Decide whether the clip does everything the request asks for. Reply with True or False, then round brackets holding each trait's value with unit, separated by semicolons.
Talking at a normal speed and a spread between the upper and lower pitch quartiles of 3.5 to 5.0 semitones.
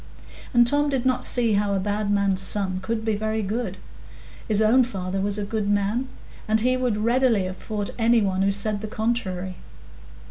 False (190 wpm; 2.8 semitones)